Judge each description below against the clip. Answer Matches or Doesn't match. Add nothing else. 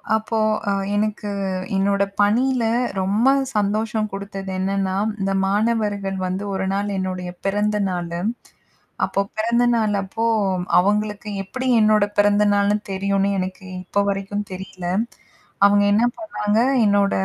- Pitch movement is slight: Matches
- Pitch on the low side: Doesn't match